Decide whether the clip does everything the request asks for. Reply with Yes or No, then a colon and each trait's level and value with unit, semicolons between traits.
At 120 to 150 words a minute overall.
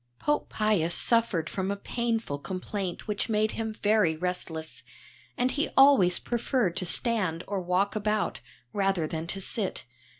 Yes: average, 145 wpm